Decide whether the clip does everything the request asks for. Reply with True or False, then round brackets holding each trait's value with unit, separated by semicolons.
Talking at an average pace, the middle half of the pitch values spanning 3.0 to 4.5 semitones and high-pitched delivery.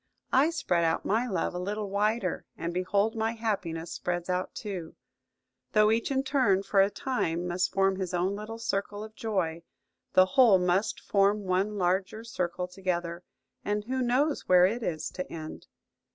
True (170 wpm; 3.5 semitones; 195 Hz)